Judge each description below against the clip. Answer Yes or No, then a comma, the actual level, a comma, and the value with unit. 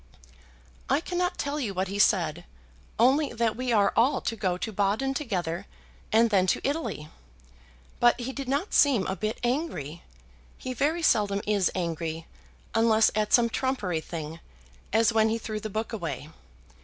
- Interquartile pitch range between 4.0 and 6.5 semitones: Yes, average, 5.2 semitones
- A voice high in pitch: Yes, high, 220 Hz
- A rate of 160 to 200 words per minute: Yes, average, 165 wpm